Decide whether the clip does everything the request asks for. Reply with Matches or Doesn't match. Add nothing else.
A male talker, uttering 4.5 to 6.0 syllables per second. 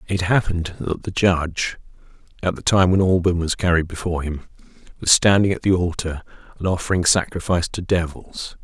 Matches